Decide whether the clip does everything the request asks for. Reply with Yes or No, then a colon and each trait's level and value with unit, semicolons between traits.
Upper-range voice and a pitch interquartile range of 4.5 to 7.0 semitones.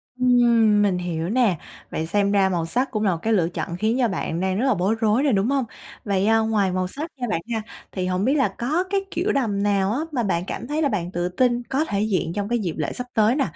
Yes: high, 210 Hz; average, 5.1 semitones